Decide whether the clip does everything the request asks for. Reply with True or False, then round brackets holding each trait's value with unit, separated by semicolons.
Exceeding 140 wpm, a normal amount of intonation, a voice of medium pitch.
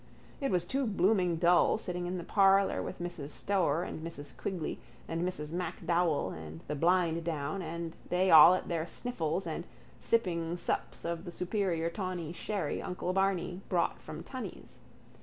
False (160 wpm; 2.1 semitones; 175 Hz)